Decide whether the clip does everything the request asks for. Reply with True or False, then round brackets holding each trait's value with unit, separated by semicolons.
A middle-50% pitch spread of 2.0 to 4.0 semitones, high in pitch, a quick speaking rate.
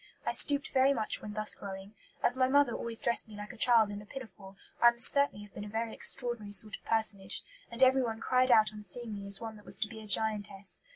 True (2.7 semitones; 220 Hz; 245 wpm)